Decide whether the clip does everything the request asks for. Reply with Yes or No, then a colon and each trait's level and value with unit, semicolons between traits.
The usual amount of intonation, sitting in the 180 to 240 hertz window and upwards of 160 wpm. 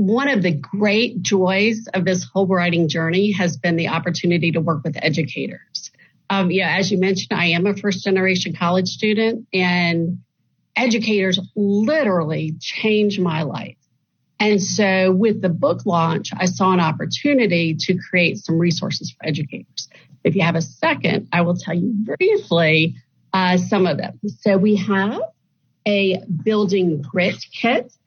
No: average, 3.2 semitones; medium, 185 Hz; average, 155 wpm